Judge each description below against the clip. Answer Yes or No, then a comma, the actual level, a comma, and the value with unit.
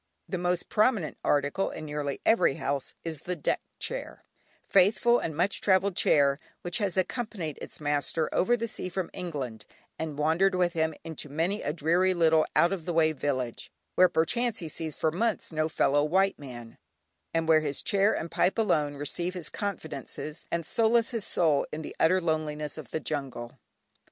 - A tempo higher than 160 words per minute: Yes, average, 180 wpm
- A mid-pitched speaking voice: Yes, medium, 165 Hz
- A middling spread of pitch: Yes, average, 3.9 semitones